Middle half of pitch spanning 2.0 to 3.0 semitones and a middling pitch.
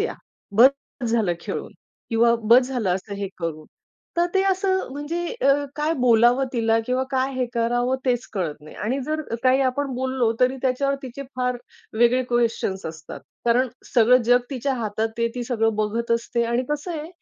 No: average, 2.7 semitones; high, 245 Hz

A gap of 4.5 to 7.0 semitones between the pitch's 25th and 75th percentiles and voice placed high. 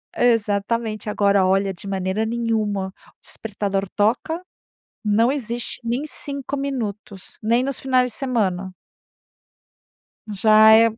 No: average, 3.2 semitones; high, 220 Hz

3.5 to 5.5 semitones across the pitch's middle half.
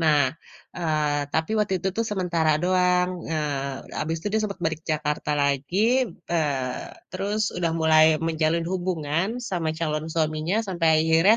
No: average, 2.9 semitones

